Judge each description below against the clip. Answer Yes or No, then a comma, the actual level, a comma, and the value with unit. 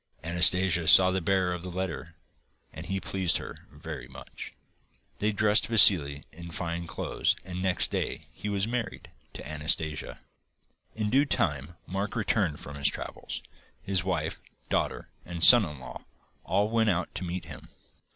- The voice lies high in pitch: No, very low, 90 Hz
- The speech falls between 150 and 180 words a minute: Yes, average, 160 wpm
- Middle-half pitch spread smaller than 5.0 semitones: Yes, average, 3.6 semitones